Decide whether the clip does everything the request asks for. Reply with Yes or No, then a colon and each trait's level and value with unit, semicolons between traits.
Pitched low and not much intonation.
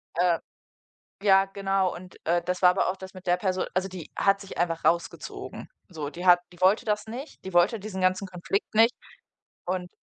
No: medium, 185 Hz; narrow, 1.7 semitones